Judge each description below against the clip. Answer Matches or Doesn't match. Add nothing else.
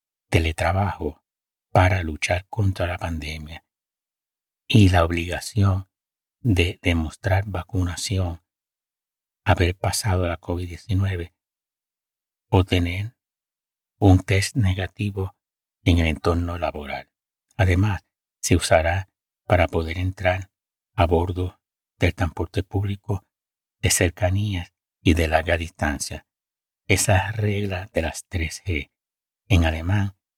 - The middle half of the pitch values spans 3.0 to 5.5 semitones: Doesn't match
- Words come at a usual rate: Doesn't match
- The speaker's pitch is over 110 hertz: Doesn't match